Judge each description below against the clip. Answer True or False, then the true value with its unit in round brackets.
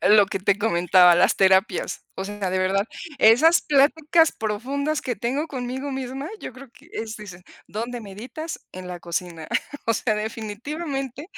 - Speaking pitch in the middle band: False (225 Hz)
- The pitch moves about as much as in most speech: False (5.8 semitones)